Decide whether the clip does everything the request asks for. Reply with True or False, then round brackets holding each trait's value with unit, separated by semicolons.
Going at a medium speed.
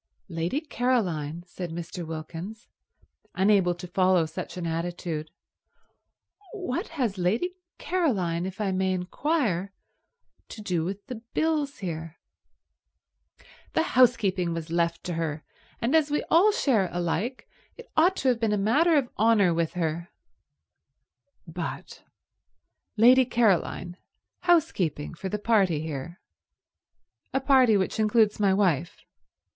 False (125 wpm)